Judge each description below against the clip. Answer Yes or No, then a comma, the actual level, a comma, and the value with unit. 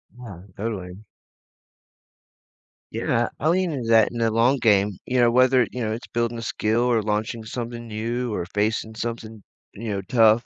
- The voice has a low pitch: Yes, low, 115 Hz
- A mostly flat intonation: Yes, narrow, 1.8 semitones